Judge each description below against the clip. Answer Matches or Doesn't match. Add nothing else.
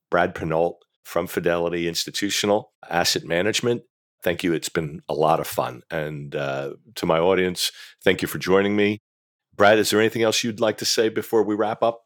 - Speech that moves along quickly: Doesn't match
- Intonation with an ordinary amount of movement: Matches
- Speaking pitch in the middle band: Doesn't match